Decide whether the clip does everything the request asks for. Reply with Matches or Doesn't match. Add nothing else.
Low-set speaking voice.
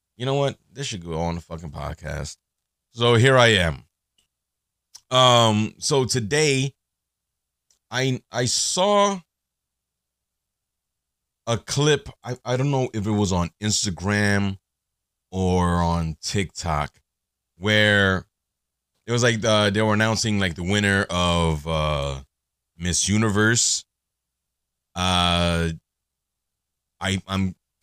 Matches